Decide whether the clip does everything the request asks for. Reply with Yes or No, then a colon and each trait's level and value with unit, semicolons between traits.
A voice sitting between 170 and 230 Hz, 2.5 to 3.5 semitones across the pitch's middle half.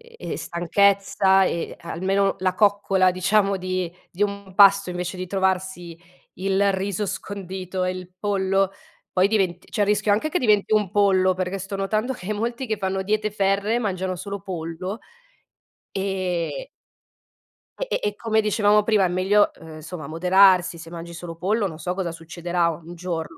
No: high, 190 Hz; narrow, 2.1 semitones